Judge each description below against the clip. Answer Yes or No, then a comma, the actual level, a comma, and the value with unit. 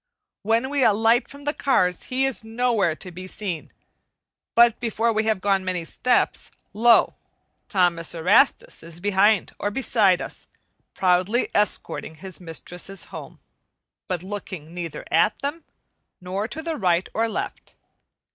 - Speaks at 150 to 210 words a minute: No, average, 140 wpm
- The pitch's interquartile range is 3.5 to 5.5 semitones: Yes, average, 4.5 semitones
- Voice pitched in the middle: No, high, 205 Hz